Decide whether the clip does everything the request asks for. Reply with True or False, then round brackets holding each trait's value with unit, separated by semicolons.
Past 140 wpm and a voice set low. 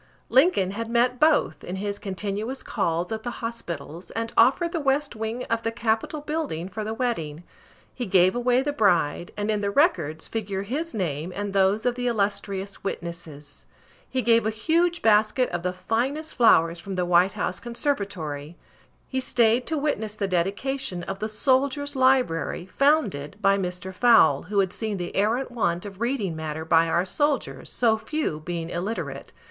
False (175 wpm; 210 Hz)